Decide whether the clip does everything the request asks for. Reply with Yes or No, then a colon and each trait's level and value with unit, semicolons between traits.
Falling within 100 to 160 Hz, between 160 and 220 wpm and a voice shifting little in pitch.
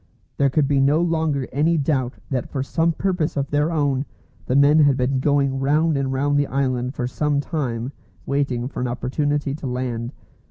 Yes: medium, 140 Hz; average, 190 wpm; narrow, 2.3 semitones